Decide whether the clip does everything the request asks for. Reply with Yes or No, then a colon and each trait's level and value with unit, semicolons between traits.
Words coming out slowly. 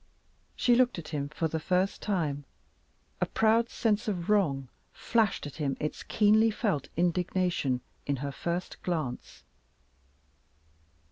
Yes: slow, 130 wpm